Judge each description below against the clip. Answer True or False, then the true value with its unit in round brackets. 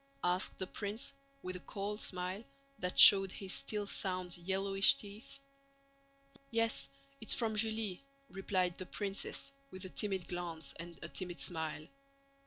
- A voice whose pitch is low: False (190 Hz)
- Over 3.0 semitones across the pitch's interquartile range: False (2.5 semitones)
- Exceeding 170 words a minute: False (140 wpm)